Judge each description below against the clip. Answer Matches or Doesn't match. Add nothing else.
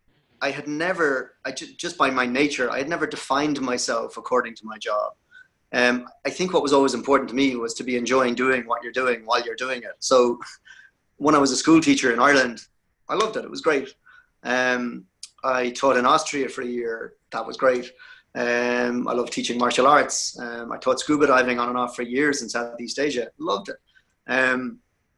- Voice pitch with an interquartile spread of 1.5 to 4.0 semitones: Matches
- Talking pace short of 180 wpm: Doesn't match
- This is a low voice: Matches